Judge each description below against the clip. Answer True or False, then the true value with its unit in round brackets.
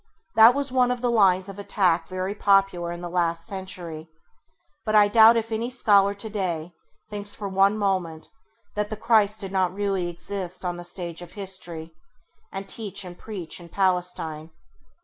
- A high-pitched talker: True (195 Hz)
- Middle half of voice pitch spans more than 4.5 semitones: False (3.0 semitones)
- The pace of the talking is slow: False (170 wpm)